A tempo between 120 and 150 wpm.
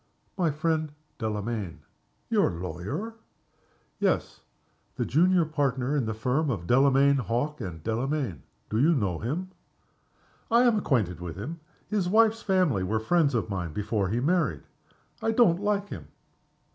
Yes: average, 145 wpm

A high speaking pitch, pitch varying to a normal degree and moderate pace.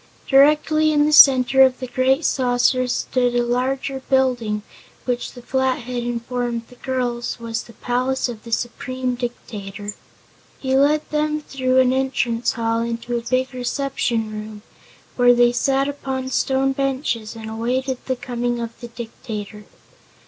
No: very high, 250 Hz; narrow, 2.1 semitones; average, 150 wpm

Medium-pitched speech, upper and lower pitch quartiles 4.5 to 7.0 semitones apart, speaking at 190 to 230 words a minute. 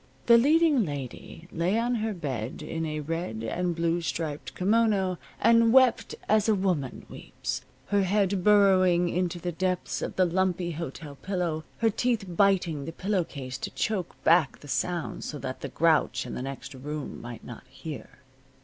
No: medium, 175 Hz; average, 5.1 semitones; average, 170 wpm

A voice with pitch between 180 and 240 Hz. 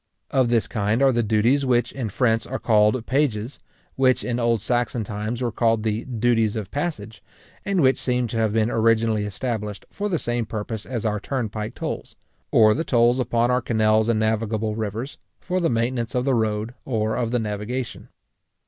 No: low, 115 Hz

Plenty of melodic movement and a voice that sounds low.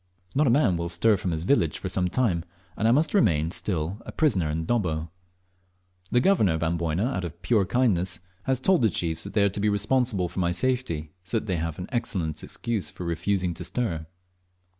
Yes: wide, 5.9 semitones; very low, 95 Hz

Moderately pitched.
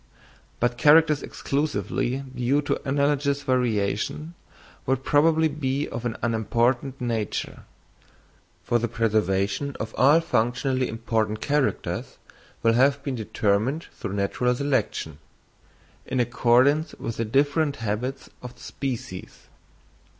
No: low, 125 Hz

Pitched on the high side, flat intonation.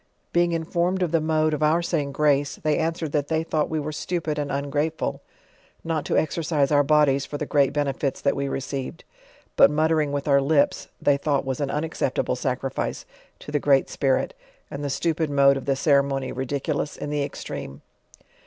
No: medium, 145 Hz; narrow, 2.2 semitones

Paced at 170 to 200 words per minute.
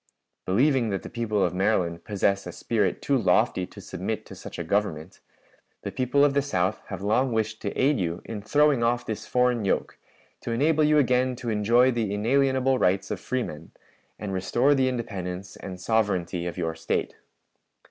Yes: average, 180 wpm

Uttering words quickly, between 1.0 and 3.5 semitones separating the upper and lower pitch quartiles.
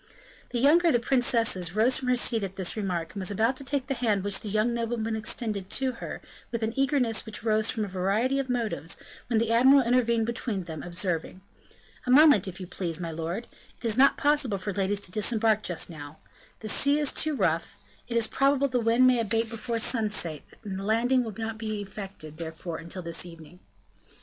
No: fast, 210 wpm; average, 4.4 semitones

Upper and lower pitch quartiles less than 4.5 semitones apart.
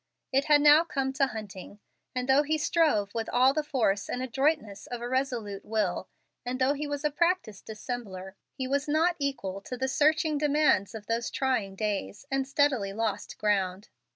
No: wide, 5.6 semitones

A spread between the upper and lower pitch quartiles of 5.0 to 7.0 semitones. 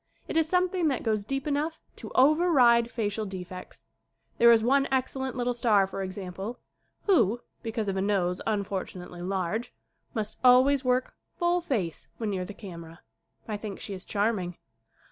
Yes: average, 5.3 semitones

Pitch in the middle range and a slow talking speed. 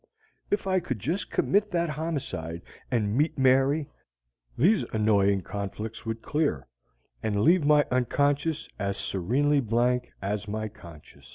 No: low, 125 Hz; slow, 130 wpm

